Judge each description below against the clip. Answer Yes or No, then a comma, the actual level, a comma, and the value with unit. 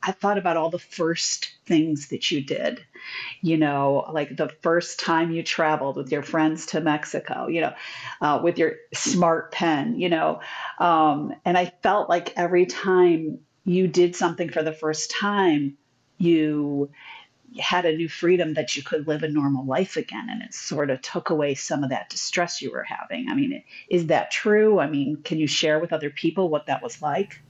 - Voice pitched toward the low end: No, medium, 165 Hz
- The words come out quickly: No, average, 195 wpm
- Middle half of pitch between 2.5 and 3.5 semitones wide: Yes, average, 3.0 semitones